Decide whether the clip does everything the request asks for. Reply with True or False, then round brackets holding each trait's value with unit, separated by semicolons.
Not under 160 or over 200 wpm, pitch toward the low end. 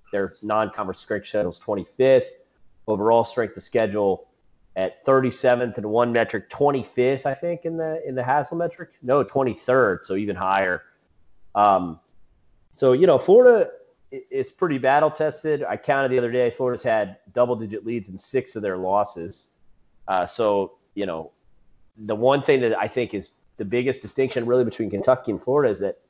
True (170 wpm; 125 Hz)